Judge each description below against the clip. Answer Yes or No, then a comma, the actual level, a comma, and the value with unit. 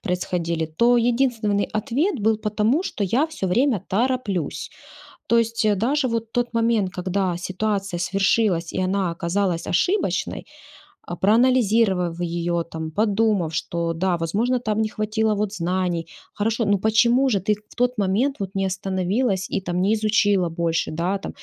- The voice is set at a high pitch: Yes, high, 205 Hz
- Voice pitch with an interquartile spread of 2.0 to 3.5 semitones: No, average, 4.2 semitones